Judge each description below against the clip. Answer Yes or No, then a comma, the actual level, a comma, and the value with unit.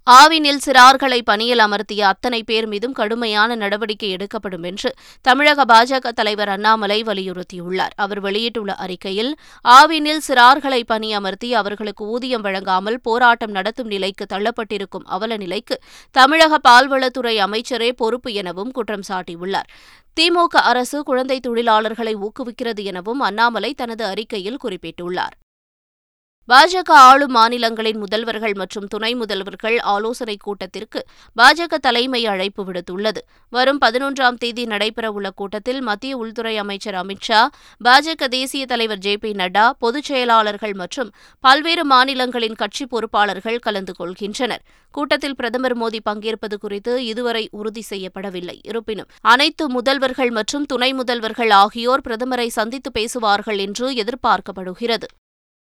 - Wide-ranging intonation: No, average, 3.5 semitones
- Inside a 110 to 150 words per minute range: Yes, average, 115 wpm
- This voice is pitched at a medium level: No, high, 225 Hz